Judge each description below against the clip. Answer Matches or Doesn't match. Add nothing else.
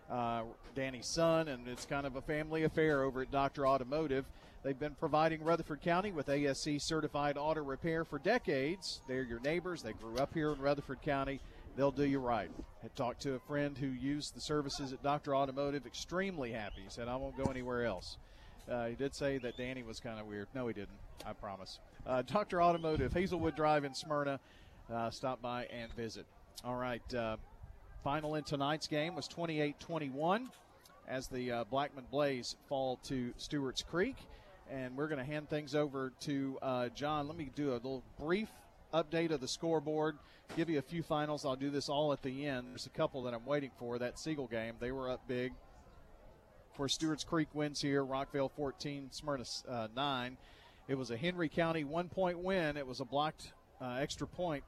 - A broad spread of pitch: Doesn't match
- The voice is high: Doesn't match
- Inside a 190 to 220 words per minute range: Matches